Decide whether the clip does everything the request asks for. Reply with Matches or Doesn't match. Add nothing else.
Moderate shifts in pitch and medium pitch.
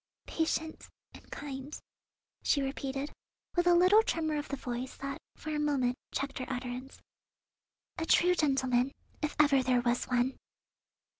Doesn't match